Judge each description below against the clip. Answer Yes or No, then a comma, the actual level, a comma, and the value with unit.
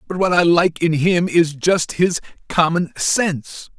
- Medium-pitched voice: Yes, medium, 170 Hz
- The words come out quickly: No, average, 175 wpm